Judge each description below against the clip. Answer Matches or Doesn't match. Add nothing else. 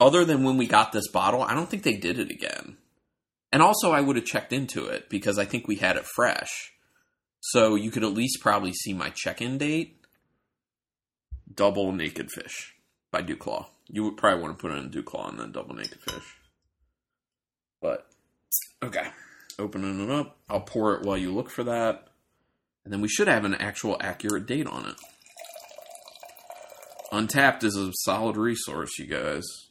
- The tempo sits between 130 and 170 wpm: Doesn't match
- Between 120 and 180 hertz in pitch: Doesn't match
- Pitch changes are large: Matches